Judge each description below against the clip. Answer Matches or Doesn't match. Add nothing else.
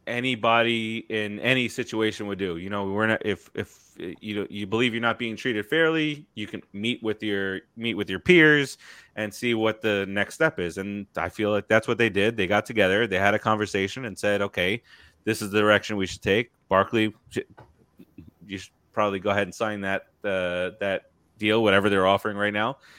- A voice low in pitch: Matches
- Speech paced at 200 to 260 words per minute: Matches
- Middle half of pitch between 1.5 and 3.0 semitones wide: Matches